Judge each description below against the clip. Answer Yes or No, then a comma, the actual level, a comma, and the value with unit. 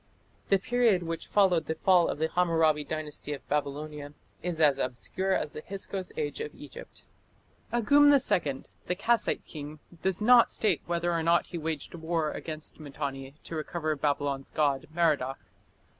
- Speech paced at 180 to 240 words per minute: No, average, 160 wpm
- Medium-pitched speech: Yes, medium, 160 Hz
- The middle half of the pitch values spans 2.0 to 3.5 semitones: No, average, 4.2 semitones